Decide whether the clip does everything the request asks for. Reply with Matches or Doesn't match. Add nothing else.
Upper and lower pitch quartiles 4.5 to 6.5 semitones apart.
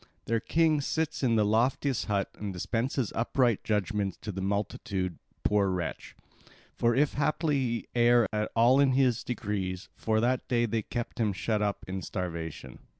Doesn't match